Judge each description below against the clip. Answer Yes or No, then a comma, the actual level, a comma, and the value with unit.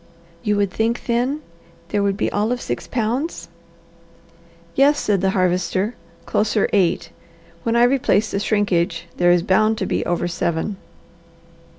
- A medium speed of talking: Yes, average, 150 wpm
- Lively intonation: No, average, 4.1 semitones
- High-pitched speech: Yes, high, 205 Hz